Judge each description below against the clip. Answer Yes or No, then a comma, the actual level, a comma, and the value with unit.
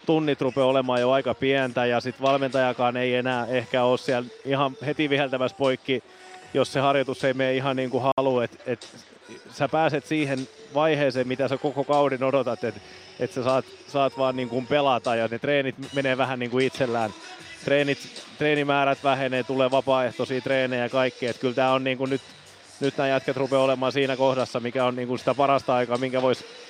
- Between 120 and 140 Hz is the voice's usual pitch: Yes, low, 130 Hz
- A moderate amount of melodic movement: No, narrow, 1.4 semitones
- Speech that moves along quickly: Yes, fast, 195 wpm